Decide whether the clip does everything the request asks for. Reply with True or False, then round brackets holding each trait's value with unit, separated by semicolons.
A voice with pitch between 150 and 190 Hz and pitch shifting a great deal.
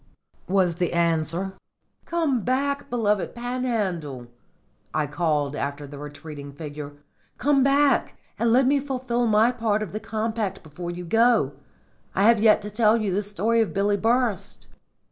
False (210 Hz; 6.1 semitones)